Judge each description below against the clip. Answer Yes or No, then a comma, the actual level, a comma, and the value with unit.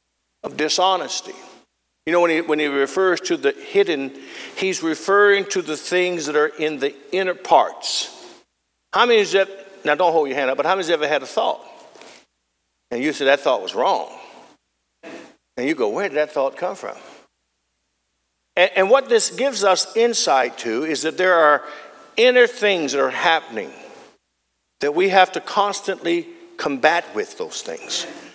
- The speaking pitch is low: No, medium, 175 Hz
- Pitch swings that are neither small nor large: No, wide, 6.4 semitones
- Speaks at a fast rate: No, average, 180 wpm